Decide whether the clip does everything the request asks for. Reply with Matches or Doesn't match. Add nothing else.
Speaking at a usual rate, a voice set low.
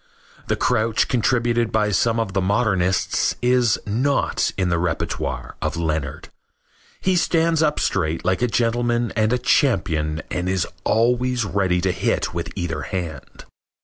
Matches